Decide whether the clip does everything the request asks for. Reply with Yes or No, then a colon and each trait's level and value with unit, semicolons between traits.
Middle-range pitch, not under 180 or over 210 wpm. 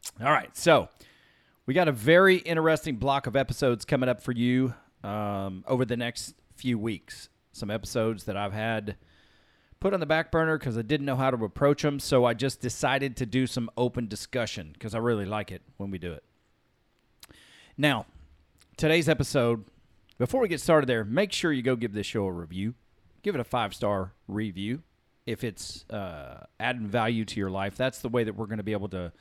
No: low, 120 Hz; average, 200 wpm